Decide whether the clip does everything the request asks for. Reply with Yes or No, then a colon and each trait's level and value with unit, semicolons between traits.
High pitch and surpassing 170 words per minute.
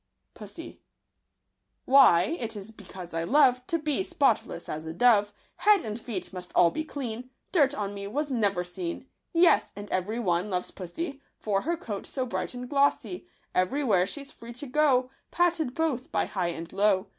Yes: high, 235 Hz; average, 180 wpm